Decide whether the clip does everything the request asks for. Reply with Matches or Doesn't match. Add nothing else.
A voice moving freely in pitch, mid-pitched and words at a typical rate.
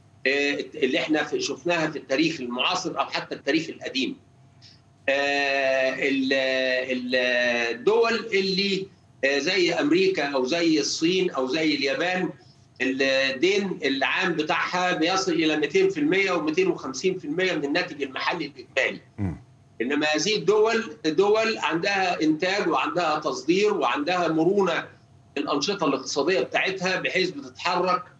Matches